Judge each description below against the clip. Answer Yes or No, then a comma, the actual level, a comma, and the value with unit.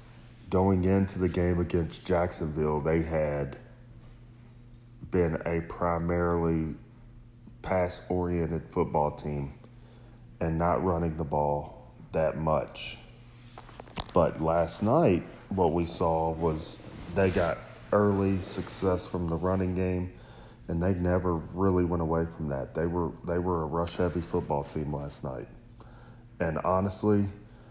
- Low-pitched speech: Yes, very low, 90 Hz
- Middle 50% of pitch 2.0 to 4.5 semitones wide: No, average, 5.3 semitones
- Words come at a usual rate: No, slow, 125 wpm